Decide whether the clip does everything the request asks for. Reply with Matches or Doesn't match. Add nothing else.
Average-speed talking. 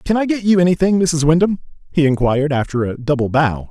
Doesn't match